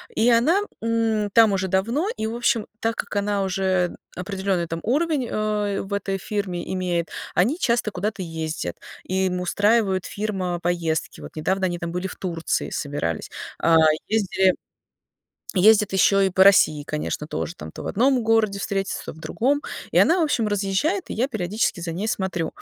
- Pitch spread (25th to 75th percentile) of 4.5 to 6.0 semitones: No, average, 3.7 semitones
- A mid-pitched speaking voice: No, high, 195 Hz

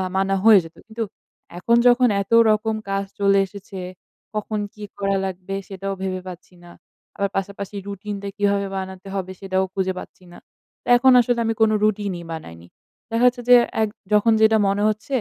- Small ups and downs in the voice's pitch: Yes, narrow, 2.2 semitones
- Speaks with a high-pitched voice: Yes, high, 200 Hz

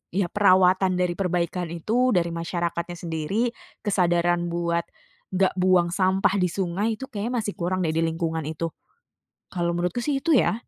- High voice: No, medium, 180 Hz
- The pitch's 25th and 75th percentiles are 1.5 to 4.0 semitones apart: Yes, narrow, 2.6 semitones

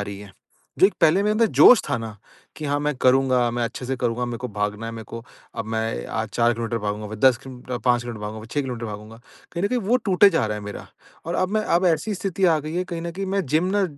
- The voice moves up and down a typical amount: No, wide, 7.3 semitones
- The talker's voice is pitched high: No, low, 125 Hz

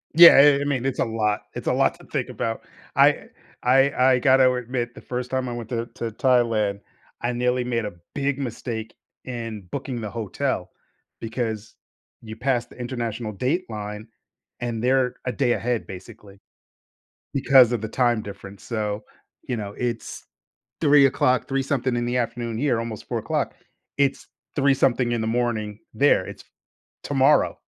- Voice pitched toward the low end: Yes, low, 120 Hz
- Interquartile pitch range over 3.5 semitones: No, average, 2.8 semitones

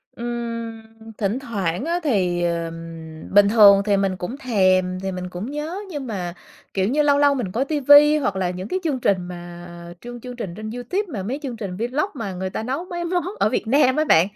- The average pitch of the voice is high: Yes, high, 220 Hz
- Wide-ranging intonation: Yes, wide, 7.1 semitones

